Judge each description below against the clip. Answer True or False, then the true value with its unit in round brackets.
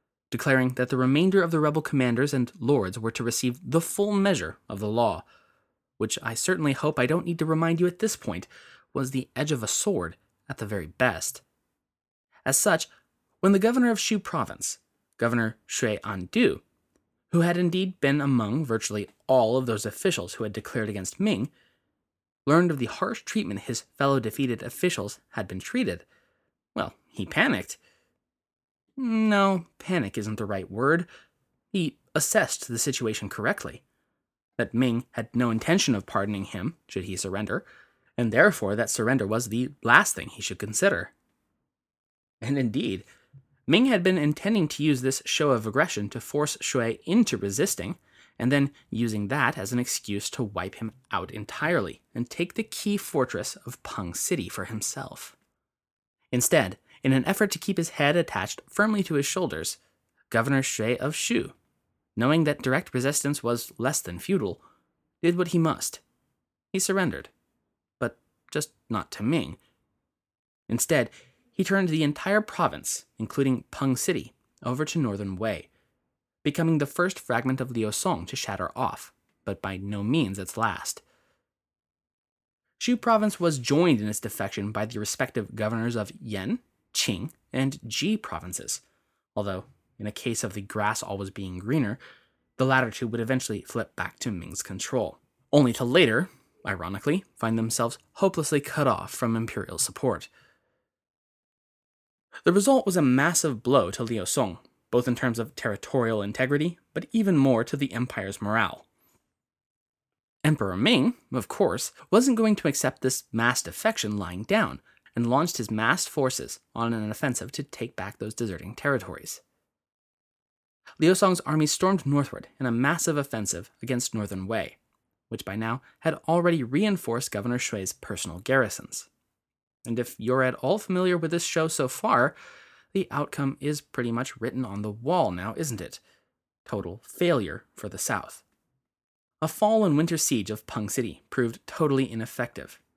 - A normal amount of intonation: False (6.5 semitones)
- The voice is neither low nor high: False (130 Hz)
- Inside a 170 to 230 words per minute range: False (160 wpm)